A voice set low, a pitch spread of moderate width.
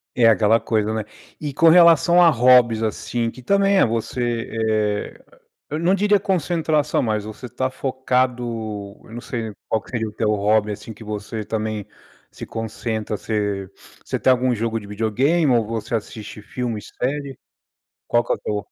Yes: low, 115 Hz; average, 3.4 semitones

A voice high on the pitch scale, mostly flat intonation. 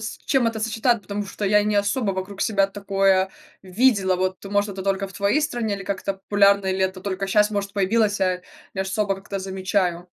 Yes: high, 200 Hz; narrow, 1.5 semitones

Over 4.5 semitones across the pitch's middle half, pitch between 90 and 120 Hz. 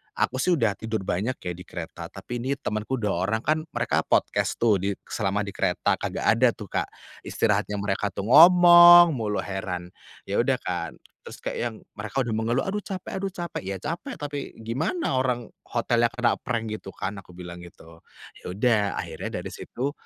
Yes: average, 5.2 semitones; low, 115 Hz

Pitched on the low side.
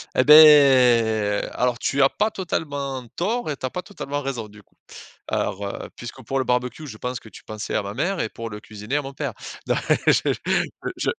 Yes: low, 130 Hz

